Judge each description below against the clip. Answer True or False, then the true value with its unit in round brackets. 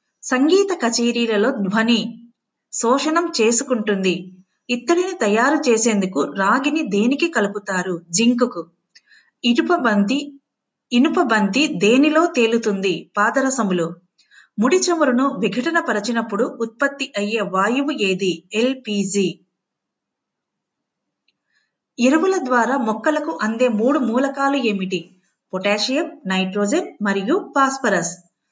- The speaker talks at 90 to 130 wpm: False (80 wpm)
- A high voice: True (235 Hz)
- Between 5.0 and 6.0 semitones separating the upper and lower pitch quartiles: True (5.3 semitones)